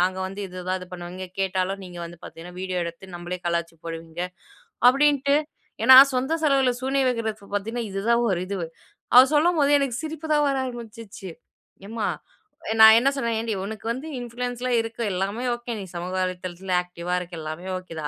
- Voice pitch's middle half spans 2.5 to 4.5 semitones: No, wide, 5.5 semitones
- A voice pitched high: Yes, high, 200 Hz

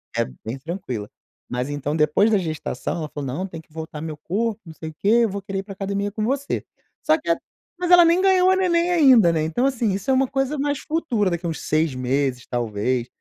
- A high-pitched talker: Yes, high, 195 Hz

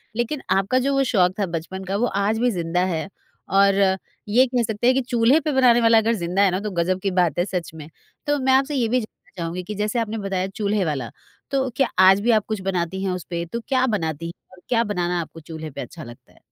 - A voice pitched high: Yes, high, 200 Hz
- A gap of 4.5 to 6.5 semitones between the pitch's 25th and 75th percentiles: Yes, average, 5.2 semitones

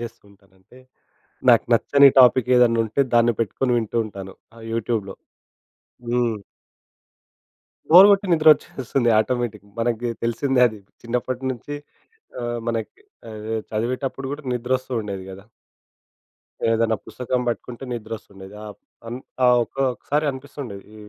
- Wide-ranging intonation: No, average, 2.8 semitones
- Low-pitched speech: Yes, low, 120 Hz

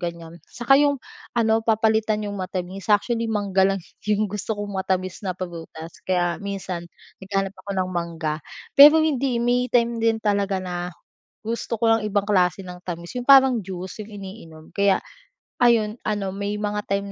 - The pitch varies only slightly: No, average, 3.3 semitones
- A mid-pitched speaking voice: No, high, 200 Hz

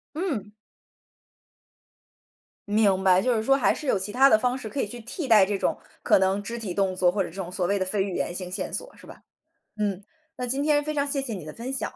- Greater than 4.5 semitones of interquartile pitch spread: Yes, wide, 5.6 semitones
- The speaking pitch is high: Yes, high, 210 Hz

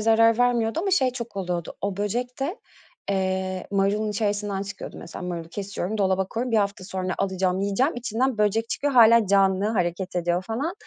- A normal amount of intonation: Yes, average, 3.4 semitones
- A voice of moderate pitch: No, high, 205 Hz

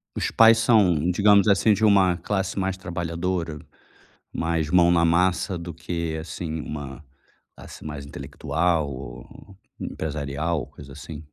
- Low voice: Yes, very low, 85 Hz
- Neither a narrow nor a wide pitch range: Yes, average, 3.5 semitones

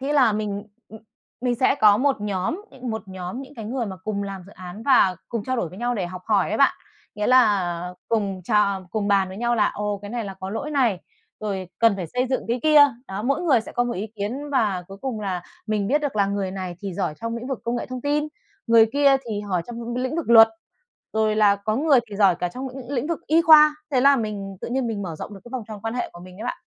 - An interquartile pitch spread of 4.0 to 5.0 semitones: Yes, average, 4.5 semitones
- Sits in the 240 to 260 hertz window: No, high, 220 Hz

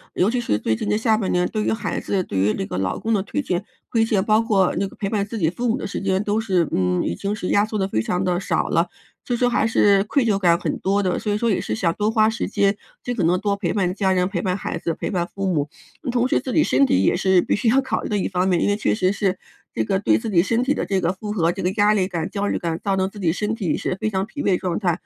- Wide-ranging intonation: No, average, 3.2 semitones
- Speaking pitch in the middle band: No, high, 195 Hz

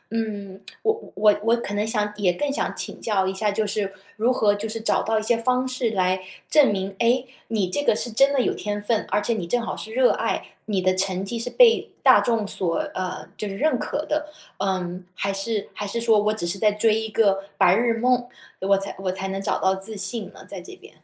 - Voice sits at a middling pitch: No, high, 210 Hz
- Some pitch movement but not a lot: Yes, average, 3.1 semitones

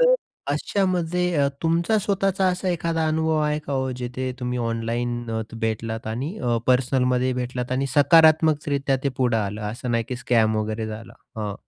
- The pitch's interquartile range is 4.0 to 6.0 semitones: Yes, average, 5.3 semitones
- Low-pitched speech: Yes, low, 130 Hz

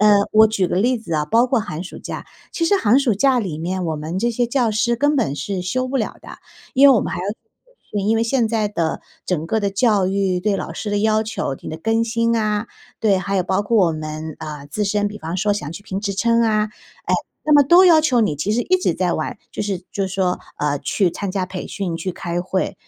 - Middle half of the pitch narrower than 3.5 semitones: No, average, 4.2 semitones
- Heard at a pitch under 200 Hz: No, high, 205 Hz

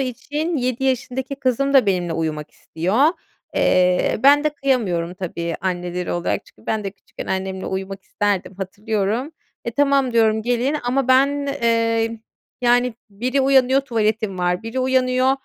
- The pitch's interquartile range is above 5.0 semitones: Yes, wide, 5.5 semitones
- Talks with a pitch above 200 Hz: Yes, high, 230 Hz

